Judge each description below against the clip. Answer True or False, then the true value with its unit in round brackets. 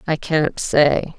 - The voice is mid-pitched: True (150 Hz)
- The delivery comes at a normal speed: True (150 wpm)